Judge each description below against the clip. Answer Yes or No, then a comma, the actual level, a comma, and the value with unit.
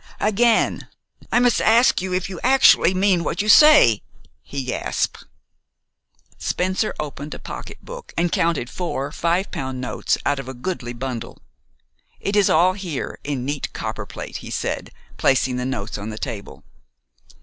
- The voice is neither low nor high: Yes, medium, 170 Hz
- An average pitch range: No, wide, 6.8 semitones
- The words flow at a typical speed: Yes, average, 150 wpm